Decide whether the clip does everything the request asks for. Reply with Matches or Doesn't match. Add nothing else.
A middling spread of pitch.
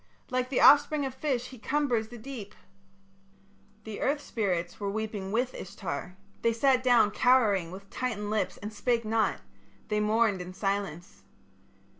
Matches